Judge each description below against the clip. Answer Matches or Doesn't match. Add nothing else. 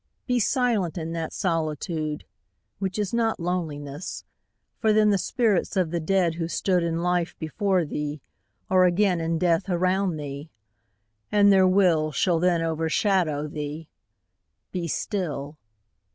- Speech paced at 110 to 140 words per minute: Matches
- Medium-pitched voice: Matches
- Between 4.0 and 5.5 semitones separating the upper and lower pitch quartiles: Doesn't match